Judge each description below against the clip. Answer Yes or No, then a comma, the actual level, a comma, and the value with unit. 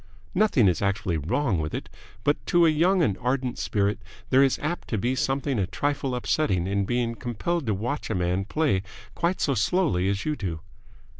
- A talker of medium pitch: No, low, 120 Hz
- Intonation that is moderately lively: No, wide, 7.0 semitones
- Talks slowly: No, average, 195 wpm